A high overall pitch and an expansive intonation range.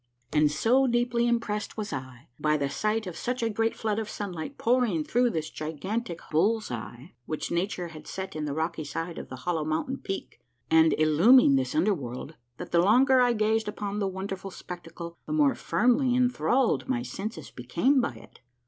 Yes: high, 195 Hz; wide, 7.0 semitones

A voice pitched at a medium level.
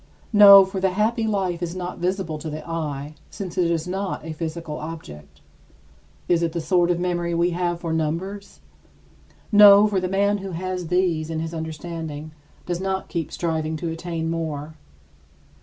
Yes: medium, 170 Hz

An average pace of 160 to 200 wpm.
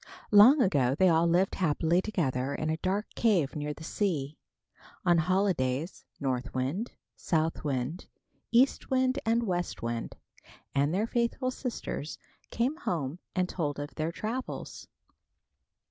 No: slow, 135 wpm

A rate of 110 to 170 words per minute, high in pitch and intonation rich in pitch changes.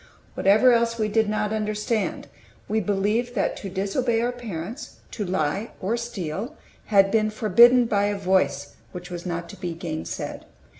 No: average, 160 wpm; high, 210 Hz; average, 3.7 semitones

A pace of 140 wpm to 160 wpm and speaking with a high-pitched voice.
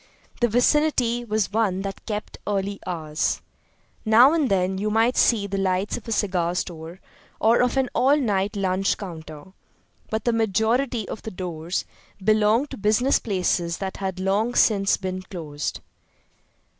Yes: average, 155 wpm; high, 200 Hz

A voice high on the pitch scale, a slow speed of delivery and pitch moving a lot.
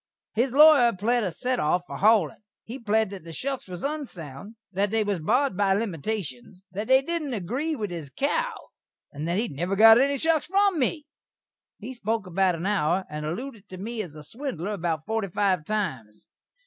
No: high, 210 Hz; average, 190 wpm; wide, 6.2 semitones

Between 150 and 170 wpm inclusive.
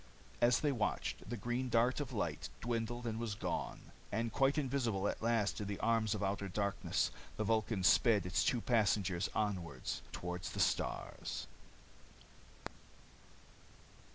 No: average, 140 wpm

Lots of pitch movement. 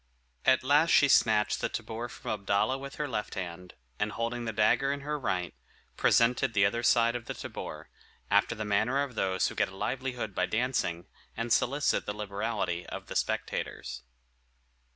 No: average, 4.2 semitones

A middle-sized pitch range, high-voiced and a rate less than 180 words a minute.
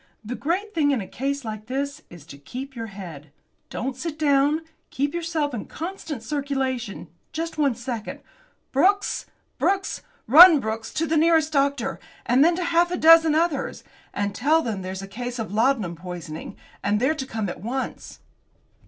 No: wide, 6.3 semitones; very high, 270 Hz; average, 170 wpm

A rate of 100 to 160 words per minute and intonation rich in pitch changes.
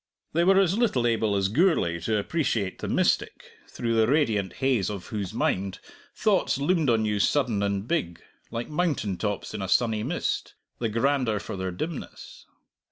No: average, 170 wpm; wide, 6.6 semitones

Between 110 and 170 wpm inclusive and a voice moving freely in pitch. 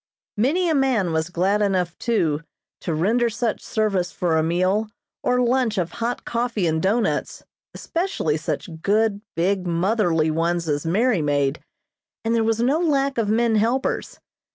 Yes: average, 155 wpm; wide, 5.8 semitones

